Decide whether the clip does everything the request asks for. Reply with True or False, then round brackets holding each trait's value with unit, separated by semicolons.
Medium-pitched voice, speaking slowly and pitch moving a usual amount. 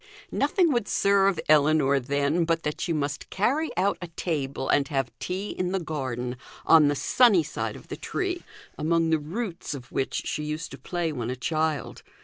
False (155 Hz; 185 wpm; 4.6 semitones)